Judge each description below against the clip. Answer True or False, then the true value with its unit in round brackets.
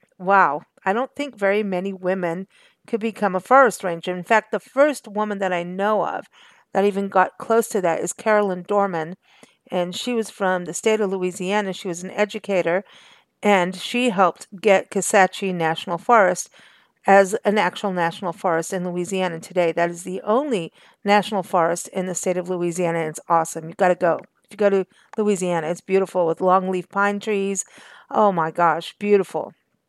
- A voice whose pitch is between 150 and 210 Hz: True (190 Hz)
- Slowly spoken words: False (180 wpm)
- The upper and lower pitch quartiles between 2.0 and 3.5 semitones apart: True (2.8 semitones)